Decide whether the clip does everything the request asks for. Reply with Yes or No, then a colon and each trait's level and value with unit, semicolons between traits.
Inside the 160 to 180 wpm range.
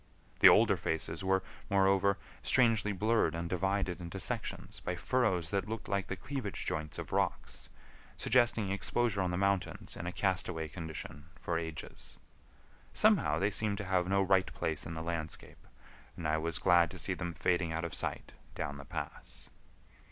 Yes: average, 170 wpm